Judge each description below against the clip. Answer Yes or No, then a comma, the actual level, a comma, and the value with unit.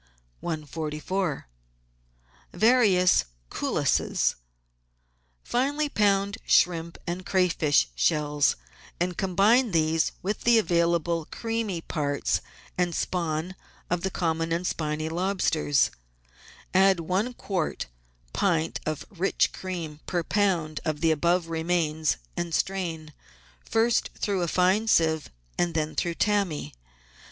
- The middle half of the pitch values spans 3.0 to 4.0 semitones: Yes, average, 3.5 semitones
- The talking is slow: Yes, slow, 110 wpm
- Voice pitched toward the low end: No, medium, 175 Hz